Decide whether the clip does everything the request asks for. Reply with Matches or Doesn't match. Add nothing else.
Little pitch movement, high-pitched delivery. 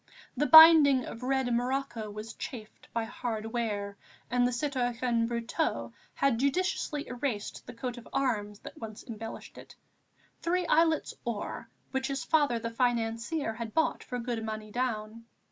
Doesn't match